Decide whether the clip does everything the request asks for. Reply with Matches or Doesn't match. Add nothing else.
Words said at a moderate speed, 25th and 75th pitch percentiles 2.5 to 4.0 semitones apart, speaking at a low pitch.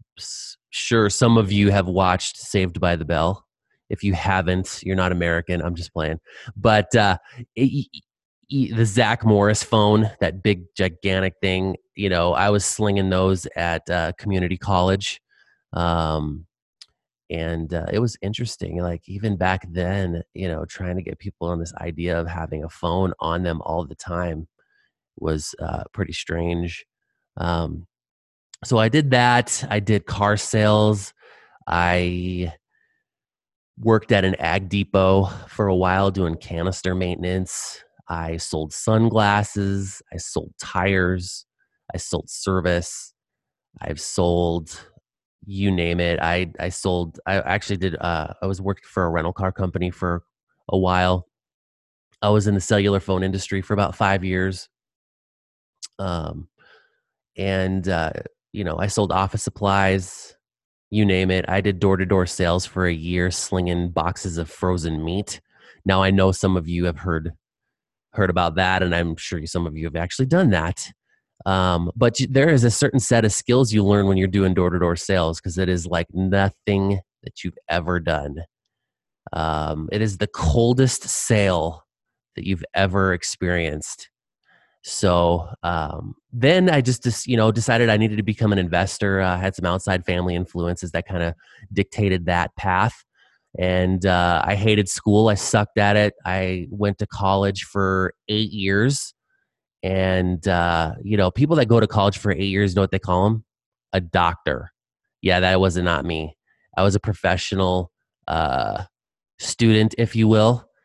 Matches